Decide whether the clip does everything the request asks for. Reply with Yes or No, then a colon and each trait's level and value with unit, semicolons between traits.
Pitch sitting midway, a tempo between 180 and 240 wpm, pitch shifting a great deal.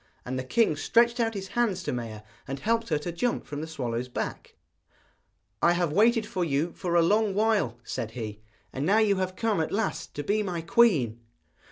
Yes: medium, 175 Hz; fast, 205 wpm; wide, 7.8 semitones